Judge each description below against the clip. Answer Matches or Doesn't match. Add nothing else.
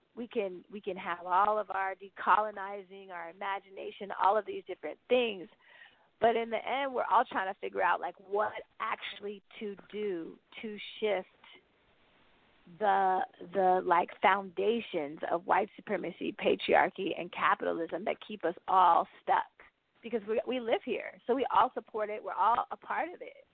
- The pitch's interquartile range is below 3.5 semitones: Matches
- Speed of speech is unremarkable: Matches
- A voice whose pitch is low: Doesn't match